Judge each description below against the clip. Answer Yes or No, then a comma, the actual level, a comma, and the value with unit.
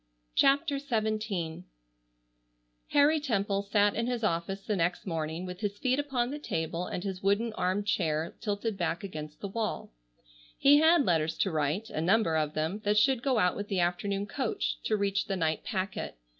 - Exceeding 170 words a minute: Yes, average, 180 wpm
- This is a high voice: Yes, high, 200 Hz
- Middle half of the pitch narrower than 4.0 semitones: No, average, 4.7 semitones